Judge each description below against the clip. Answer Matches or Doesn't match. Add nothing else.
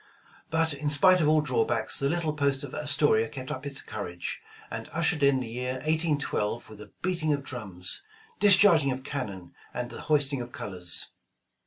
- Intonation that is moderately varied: Matches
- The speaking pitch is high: Doesn't match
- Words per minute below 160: Doesn't match